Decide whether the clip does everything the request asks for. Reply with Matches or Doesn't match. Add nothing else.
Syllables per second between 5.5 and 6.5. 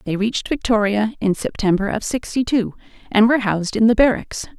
Matches